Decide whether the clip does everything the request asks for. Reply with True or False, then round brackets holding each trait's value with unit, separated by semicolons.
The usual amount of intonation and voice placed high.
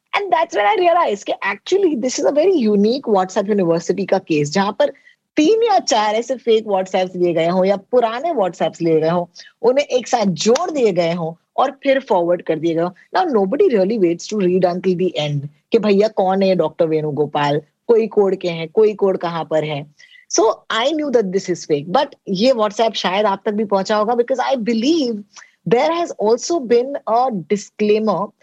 False (6.1 semitones; 210 Hz)